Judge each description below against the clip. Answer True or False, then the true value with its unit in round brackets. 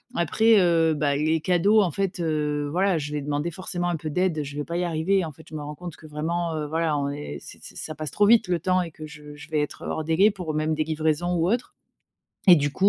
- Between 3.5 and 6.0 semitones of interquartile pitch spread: False (2.9 semitones)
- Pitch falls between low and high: True (160 Hz)